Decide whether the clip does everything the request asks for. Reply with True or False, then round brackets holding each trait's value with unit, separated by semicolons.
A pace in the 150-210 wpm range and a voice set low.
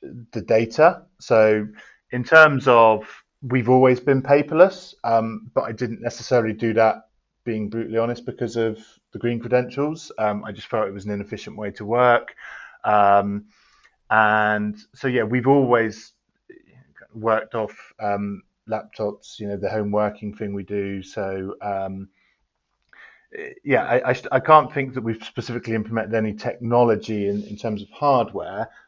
True (155 wpm; 115 Hz)